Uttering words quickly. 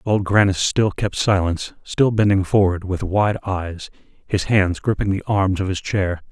No: average, 180 wpm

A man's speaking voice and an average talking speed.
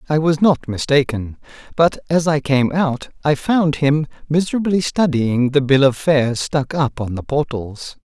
Yes: male; average, 170 wpm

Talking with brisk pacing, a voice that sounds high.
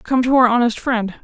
Yes: fast, 245 wpm; high, 240 Hz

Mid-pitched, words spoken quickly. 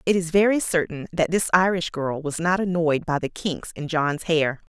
Yes: medium, 165 Hz; fast, 215 wpm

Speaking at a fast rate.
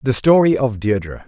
No: average, 190 wpm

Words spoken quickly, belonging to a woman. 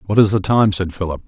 No: fast, 285 wpm; male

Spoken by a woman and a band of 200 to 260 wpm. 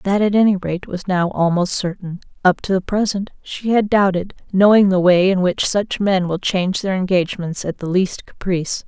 Yes: female; fast, 205 wpm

